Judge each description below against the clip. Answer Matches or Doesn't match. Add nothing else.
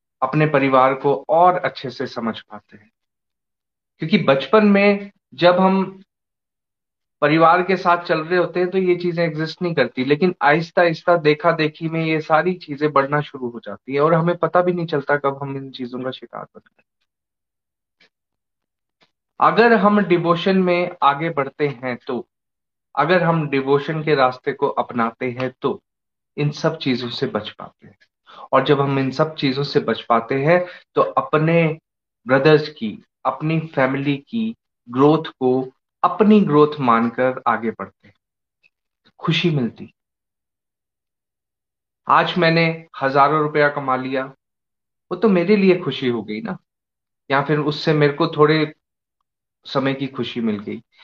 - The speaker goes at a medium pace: Matches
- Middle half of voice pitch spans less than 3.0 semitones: Doesn't match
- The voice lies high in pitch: Doesn't match